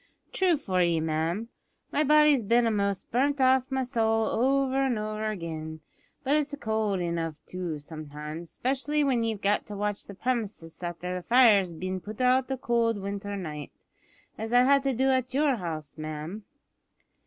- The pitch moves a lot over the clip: Yes, wide, 6.9 semitones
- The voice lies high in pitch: Yes, high, 215 Hz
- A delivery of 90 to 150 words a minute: No, average, 175 wpm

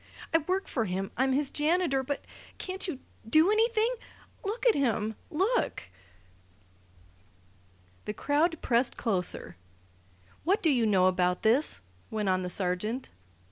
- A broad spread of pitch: Yes, wide, 8.9 semitones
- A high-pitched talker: Yes, very high, 265 Hz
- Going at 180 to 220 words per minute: No, slow, 135 wpm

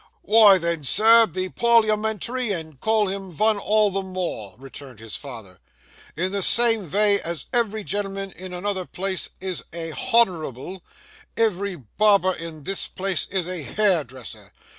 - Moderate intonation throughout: Yes, average, 4.4 semitones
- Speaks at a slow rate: No, average, 145 wpm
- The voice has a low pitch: No, high, 190 Hz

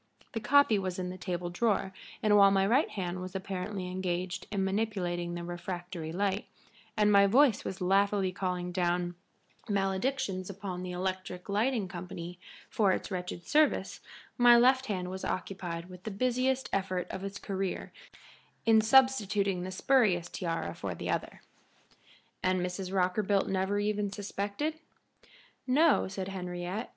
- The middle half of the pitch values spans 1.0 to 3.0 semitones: Yes, narrow, 2.5 semitones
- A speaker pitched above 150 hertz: Yes, high, 190 Hz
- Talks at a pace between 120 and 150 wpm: Yes, average, 145 wpm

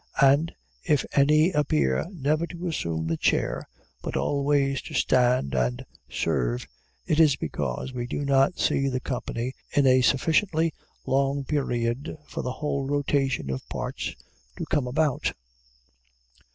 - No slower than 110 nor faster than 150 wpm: Yes, average, 140 wpm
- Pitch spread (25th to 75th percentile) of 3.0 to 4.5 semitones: Yes, average, 3.4 semitones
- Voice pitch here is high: No, low, 135 Hz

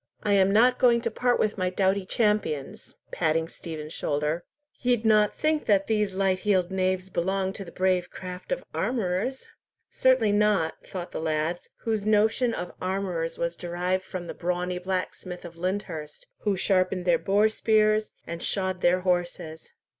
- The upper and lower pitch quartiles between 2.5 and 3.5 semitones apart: Yes, average, 3.1 semitones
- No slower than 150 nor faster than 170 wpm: Yes, average, 160 wpm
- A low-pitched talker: No, medium, 185 Hz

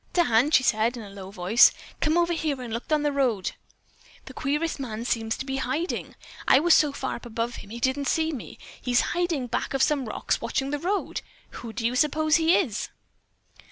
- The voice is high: Yes, very high, 265 Hz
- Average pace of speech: No, fast, 220 wpm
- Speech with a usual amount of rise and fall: Yes, average, 4.8 semitones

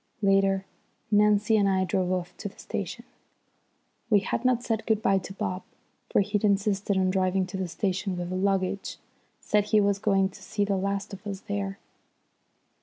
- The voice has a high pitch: Yes, high, 195 Hz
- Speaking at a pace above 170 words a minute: Yes, average, 180 wpm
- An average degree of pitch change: No, narrow, 1.4 semitones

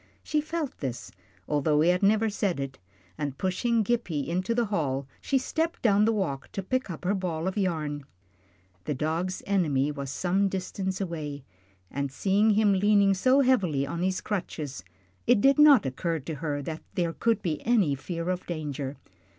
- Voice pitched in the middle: Yes, medium, 180 Hz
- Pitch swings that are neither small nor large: No, wide, 5.8 semitones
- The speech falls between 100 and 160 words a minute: No, average, 175 wpm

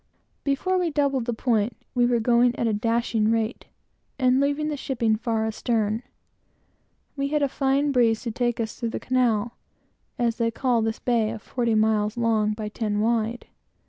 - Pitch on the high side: Yes, high, 235 Hz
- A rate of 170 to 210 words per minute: Yes, average, 175 wpm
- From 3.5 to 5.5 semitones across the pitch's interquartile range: No, narrow, 2.5 semitones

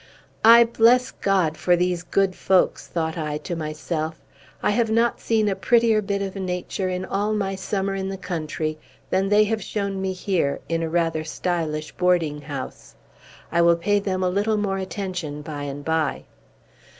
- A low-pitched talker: No, medium, 185 Hz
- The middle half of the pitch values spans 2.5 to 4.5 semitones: Yes, average, 3.7 semitones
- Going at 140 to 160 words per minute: No, average, 175 wpm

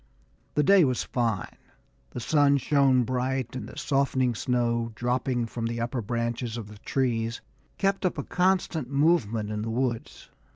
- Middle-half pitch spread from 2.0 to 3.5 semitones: Yes, average, 3.1 semitones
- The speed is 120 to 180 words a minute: Yes, average, 160 wpm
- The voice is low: Yes, low, 125 Hz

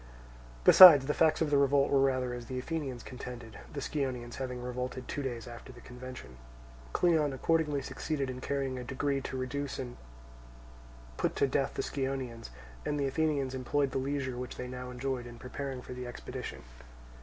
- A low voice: Yes, low, 130 Hz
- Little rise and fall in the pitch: Yes, narrow, 2.0 semitones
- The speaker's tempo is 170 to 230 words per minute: Yes, average, 180 wpm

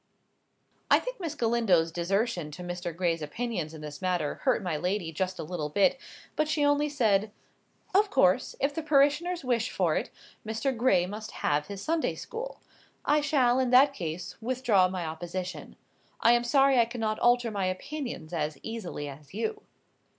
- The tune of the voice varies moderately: No, wide, 7.2 semitones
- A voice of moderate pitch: No, high, 220 Hz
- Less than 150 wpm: No, average, 170 wpm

